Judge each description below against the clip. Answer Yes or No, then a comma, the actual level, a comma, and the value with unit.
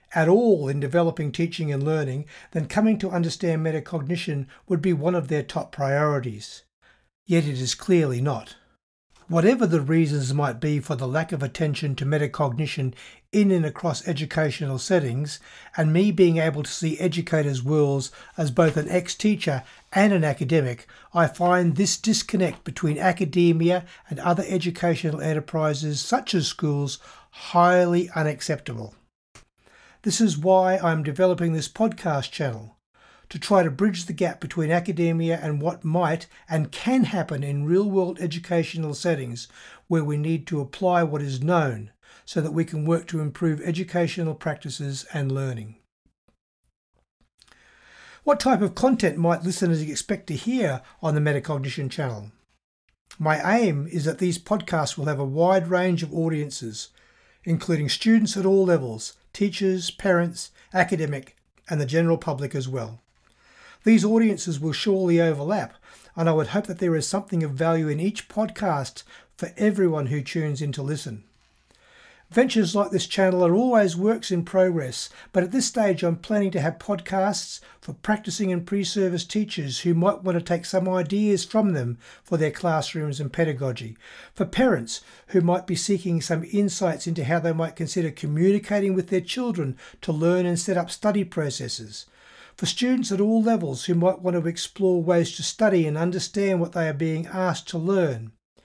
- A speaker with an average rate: Yes, average, 160 wpm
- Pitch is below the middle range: No, medium, 170 Hz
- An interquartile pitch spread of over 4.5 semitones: No, average, 3.6 semitones